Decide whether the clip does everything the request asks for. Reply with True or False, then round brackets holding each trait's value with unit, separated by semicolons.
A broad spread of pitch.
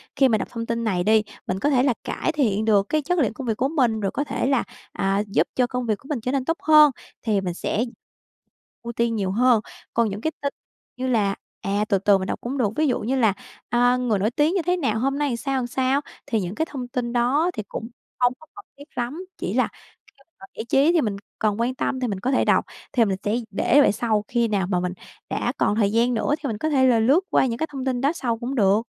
False (4.2 semitones)